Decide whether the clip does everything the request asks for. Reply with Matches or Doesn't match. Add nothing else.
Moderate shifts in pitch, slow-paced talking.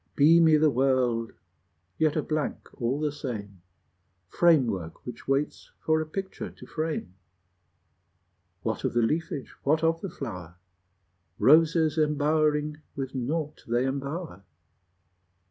Matches